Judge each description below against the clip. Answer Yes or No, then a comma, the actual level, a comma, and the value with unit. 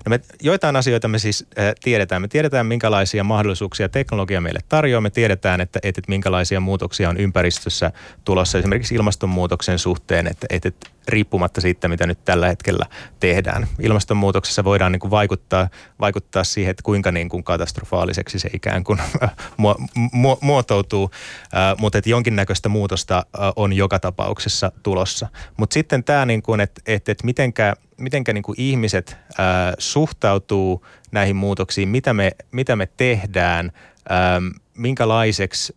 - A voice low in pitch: Yes, low, 100 Hz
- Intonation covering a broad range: No, average, 3.3 semitones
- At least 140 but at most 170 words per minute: Yes, average, 150 wpm